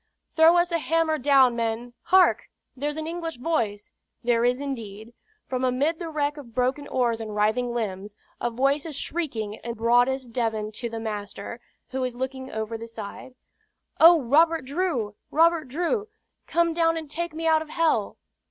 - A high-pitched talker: Yes, very high, 260 Hz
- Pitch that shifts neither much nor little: No, wide, 5.7 semitones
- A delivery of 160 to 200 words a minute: Yes, average, 170 wpm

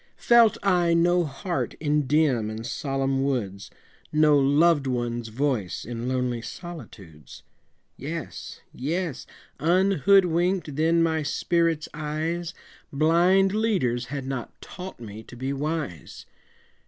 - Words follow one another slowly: Yes, slow, 115 wpm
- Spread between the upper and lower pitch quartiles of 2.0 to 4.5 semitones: No, average, 5.2 semitones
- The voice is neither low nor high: Yes, medium, 150 Hz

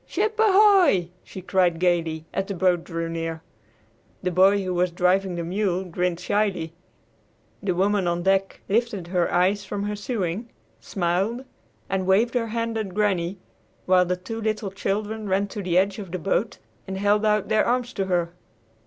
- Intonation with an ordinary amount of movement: Yes, average, 3.0 semitones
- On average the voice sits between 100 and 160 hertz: No, high, 190 Hz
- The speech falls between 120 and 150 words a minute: No, average, 175 wpm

